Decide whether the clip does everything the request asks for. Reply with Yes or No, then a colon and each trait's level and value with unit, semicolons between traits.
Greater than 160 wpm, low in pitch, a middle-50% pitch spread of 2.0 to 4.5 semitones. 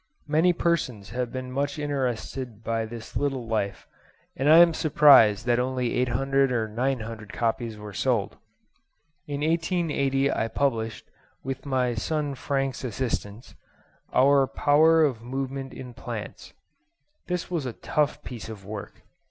No: slow, 135 wpm; low, 130 Hz; average, 3.8 semitones